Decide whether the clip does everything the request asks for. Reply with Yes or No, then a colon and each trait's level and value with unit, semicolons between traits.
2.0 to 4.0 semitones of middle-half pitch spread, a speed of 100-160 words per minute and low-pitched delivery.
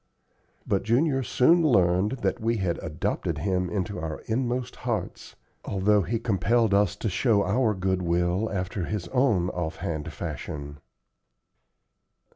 No: average, 4.6 semitones; slow, 135 wpm; low, 100 Hz